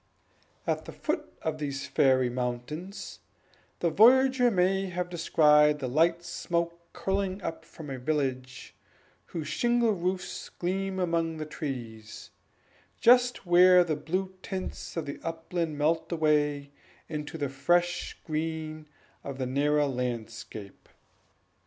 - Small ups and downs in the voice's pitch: No, average, 4.0 semitones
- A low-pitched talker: No, medium, 160 Hz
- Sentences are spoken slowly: Yes, slow, 125 wpm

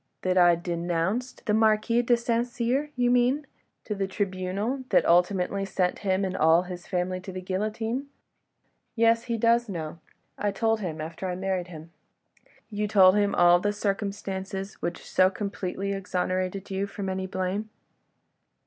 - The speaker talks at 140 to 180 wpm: Yes, average, 160 wpm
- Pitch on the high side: Yes, high, 195 Hz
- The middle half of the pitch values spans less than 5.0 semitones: Yes, average, 3.1 semitones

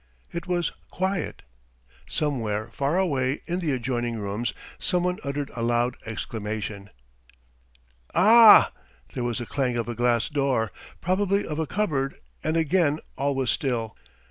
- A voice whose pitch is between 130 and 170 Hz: Yes, low, 135 Hz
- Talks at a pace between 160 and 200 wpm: No, average, 140 wpm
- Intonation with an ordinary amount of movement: No, wide, 6.3 semitones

